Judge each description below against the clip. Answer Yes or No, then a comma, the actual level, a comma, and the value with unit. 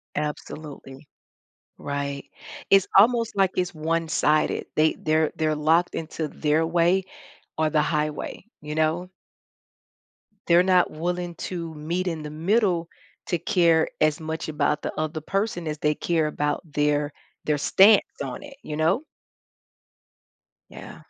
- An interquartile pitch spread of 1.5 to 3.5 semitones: Yes, average, 2.7 semitones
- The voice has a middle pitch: Yes, medium, 160 Hz